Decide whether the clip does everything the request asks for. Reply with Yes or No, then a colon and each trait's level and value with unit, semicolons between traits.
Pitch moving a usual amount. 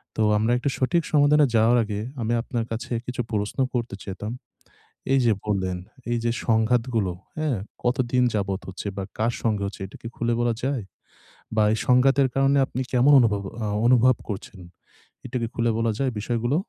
Yes: average, 3.1 semitones